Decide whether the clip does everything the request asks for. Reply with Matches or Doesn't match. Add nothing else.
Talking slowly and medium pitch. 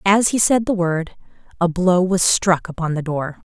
Doesn't match